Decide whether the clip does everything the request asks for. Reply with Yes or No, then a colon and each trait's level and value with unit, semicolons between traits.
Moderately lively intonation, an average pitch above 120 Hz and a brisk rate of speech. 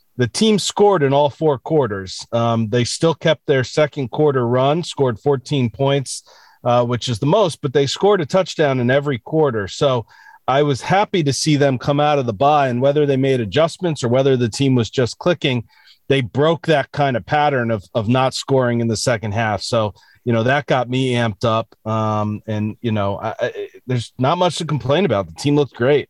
Yes: average, 4.1 semitones; low, 135 Hz; fast, 215 wpm